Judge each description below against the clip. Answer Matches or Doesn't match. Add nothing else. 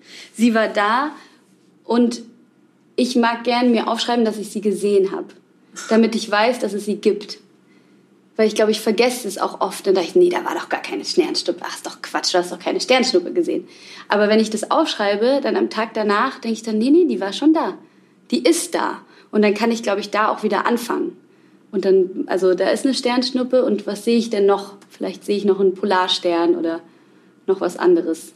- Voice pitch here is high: Matches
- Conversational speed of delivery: Doesn't match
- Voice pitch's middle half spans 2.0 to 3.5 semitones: Doesn't match